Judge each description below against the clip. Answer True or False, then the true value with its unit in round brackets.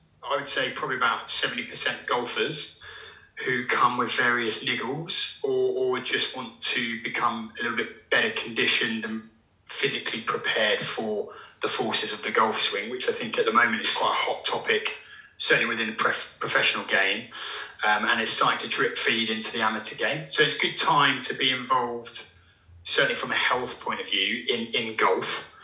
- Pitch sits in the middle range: False (115 Hz)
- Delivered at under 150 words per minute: False (185 wpm)